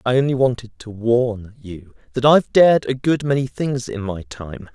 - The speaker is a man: Yes, male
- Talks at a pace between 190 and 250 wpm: Yes, average, 200 wpm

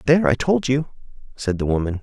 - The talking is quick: Yes, fast, 210 wpm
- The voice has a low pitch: Yes, low, 125 Hz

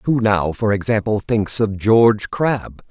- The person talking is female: No, male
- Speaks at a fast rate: No, average, 165 wpm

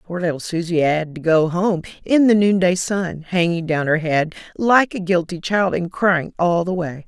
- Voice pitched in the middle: Yes, medium, 175 Hz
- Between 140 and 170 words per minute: No, fast, 205 wpm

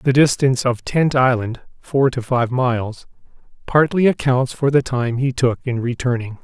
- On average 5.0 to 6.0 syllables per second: No, 4.7 syllables/s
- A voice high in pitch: No, low, 130 Hz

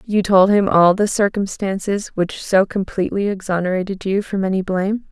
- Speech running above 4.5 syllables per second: Yes, 5.2 syllables/s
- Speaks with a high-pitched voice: Yes, high, 195 Hz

